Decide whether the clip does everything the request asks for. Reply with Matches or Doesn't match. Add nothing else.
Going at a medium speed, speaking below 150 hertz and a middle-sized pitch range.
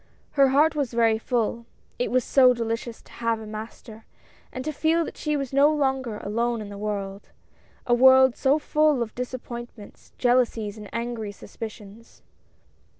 Doesn't match